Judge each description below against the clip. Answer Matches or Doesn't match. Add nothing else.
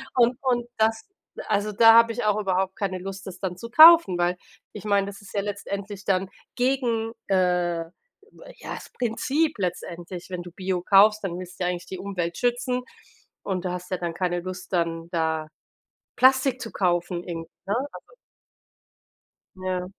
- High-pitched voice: Matches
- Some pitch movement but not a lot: Matches